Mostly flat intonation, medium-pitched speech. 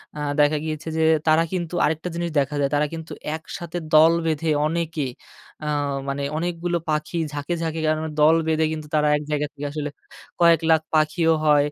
Yes: narrow, 1.6 semitones; medium, 155 Hz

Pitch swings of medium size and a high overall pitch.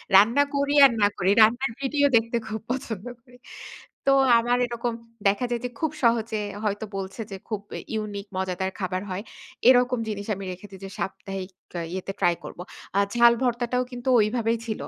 Yes: average, 3.7 semitones; high, 225 Hz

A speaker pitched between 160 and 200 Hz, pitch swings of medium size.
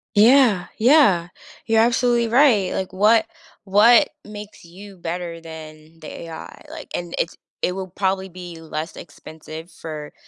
Yes: medium, 185 Hz; average, 5.0 semitones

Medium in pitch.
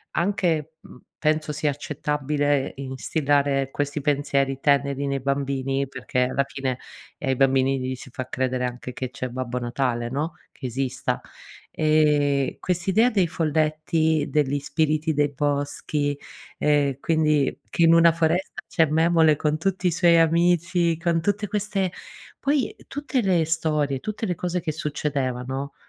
Yes: medium, 150 Hz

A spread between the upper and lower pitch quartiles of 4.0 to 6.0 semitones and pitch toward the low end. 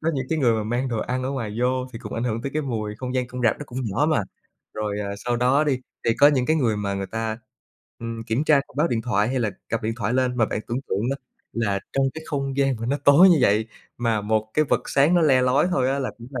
No: average, 3.6 semitones; low, 125 Hz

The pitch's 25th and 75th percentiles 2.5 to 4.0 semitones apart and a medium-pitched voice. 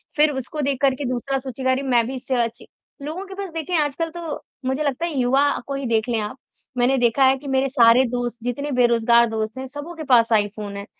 No: average, 3.1 semitones; very high, 260 Hz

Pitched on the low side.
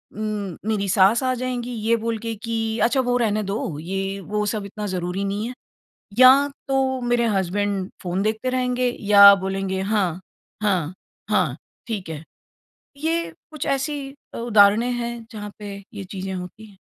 No: high, 210 Hz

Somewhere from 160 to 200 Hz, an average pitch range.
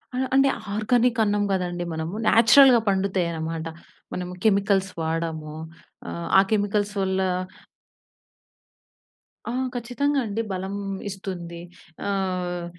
Yes: high, 195 Hz; average, 3.6 semitones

